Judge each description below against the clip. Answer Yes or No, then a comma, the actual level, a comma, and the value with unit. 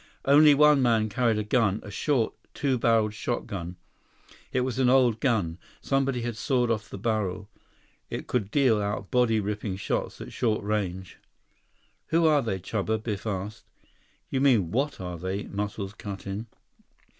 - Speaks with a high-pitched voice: No, low, 110 Hz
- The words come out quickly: No, average, 160 wpm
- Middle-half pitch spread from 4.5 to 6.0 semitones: No, average, 4.0 semitones